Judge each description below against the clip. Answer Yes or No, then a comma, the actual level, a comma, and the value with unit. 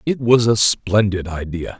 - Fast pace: No, average, 165 wpm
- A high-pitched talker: No, low, 105 Hz